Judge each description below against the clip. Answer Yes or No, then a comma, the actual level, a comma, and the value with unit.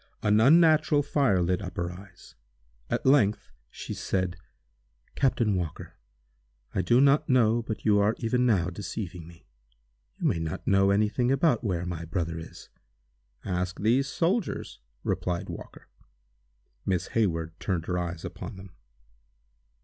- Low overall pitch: Yes, low, 100 Hz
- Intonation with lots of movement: Yes, wide, 5.8 semitones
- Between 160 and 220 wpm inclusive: No, average, 140 wpm